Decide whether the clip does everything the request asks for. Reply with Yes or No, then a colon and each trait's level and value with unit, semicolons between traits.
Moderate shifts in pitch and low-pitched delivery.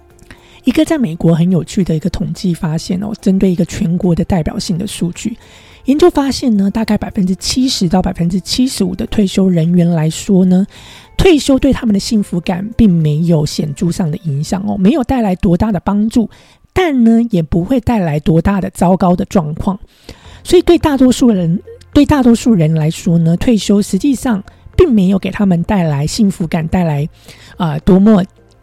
No: average, 4.5 semitones; high, 195 Hz